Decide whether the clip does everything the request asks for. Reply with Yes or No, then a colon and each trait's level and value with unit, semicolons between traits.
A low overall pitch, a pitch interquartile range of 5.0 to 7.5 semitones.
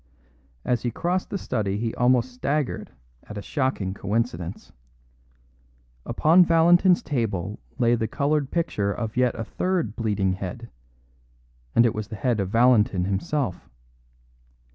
Yes: low, 120 Hz; wide, 5.5 semitones